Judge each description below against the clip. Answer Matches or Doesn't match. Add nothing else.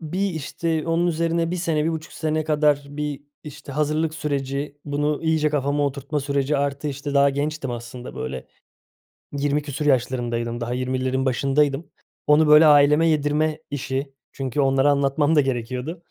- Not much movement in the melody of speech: Matches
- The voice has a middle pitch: Matches